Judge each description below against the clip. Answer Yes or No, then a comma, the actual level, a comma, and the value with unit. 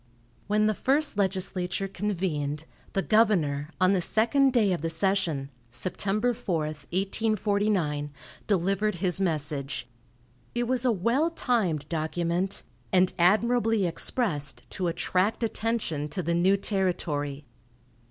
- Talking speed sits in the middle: No, slow, 120 wpm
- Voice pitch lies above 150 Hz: Yes, high, 190 Hz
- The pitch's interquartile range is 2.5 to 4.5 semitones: No, average, 4.9 semitones